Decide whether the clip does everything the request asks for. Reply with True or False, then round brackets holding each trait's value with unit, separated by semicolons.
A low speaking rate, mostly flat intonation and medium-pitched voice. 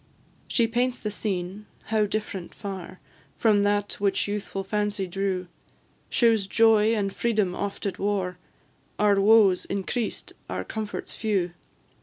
False (130 wpm; 2.0 semitones; 205 Hz)